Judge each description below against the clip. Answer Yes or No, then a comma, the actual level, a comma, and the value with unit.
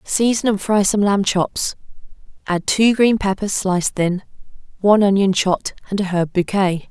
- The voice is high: Yes, high, 195 Hz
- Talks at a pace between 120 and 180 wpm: Yes, average, 165 wpm